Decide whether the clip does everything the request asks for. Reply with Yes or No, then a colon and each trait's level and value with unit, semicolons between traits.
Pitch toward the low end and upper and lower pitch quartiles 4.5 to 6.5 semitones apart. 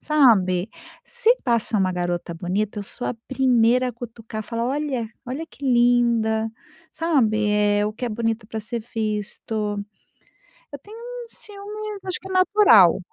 No: high, 235 Hz; wide, 5.5 semitones